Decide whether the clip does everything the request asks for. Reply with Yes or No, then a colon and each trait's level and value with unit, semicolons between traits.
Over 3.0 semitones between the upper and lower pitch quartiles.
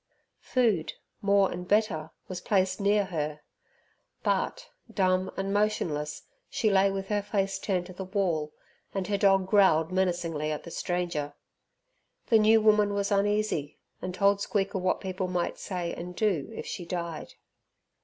No: narrow, 2.6 semitones